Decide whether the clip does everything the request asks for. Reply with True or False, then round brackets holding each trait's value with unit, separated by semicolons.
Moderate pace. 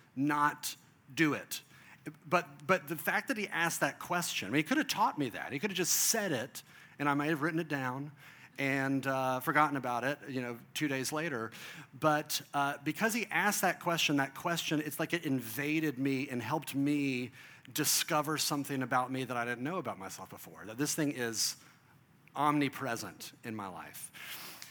True (190 wpm)